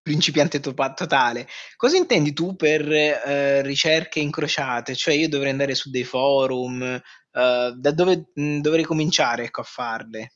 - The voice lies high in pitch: No, medium, 140 Hz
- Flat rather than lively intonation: No, average, 3.6 semitones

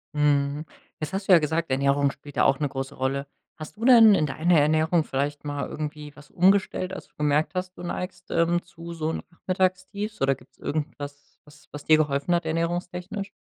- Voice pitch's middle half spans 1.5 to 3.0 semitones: No, average, 3.7 semitones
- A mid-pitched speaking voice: Yes, medium, 155 Hz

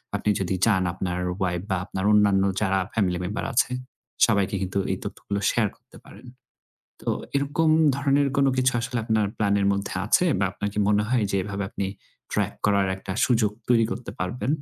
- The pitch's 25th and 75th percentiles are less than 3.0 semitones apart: No, average, 3.6 semitones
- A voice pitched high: No, low, 105 Hz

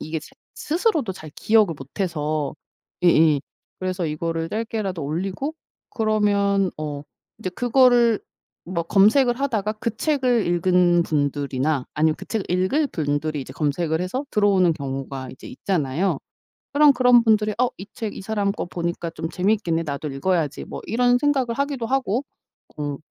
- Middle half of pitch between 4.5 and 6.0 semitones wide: No, wide, 6.4 semitones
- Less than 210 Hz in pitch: Yes, medium, 185 Hz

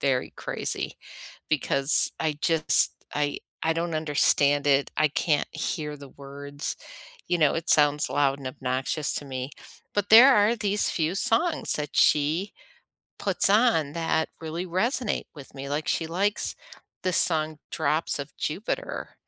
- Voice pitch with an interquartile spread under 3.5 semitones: No, average, 3.8 semitones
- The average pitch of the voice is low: No, medium, 155 Hz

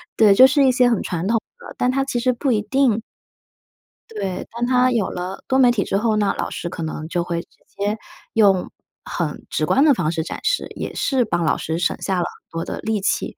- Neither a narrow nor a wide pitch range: No, wide, 5.7 semitones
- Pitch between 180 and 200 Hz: No, high, 215 Hz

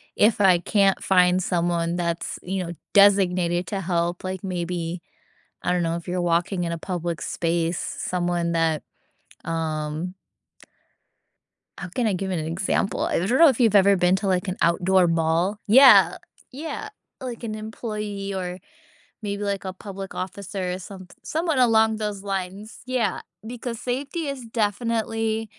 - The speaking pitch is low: No, high, 190 Hz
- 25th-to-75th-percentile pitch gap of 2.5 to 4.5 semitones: Yes, average, 3.7 semitones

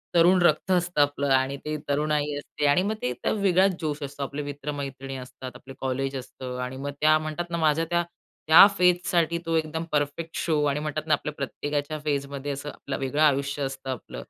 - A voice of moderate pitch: Yes, medium, 145 Hz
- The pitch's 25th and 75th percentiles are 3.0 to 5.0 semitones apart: No, narrow, 2.5 semitones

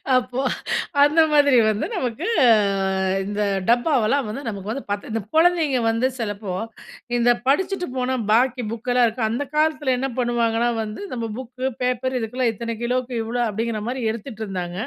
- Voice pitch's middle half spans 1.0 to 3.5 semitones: Yes, average, 2.8 semitones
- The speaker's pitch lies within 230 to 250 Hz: Yes, high, 245 Hz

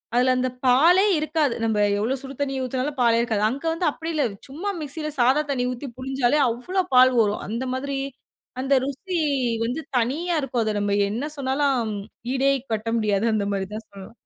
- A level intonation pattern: No, average, 3.8 semitones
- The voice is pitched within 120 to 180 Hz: No, very high, 260 Hz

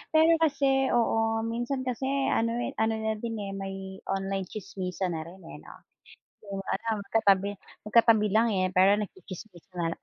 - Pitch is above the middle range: Yes, high, 210 Hz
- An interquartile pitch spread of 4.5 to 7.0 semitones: No, average, 3.2 semitones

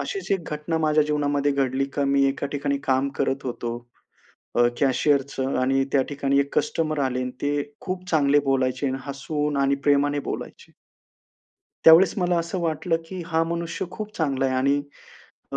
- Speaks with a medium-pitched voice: Yes, medium, 145 Hz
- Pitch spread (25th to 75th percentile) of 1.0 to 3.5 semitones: Yes, average, 2.9 semitones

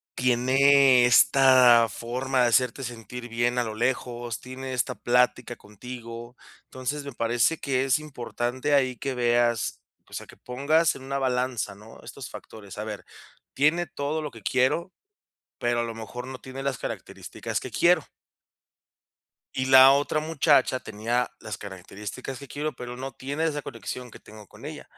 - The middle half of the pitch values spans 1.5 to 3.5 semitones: Yes, narrow, 2.4 semitones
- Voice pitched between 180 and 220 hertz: No, low, 125 Hz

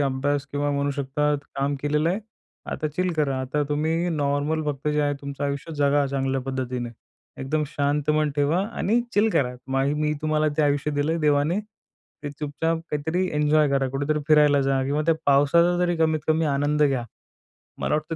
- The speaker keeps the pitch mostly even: Yes, narrow, 1.7 semitones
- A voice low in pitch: No, medium, 145 Hz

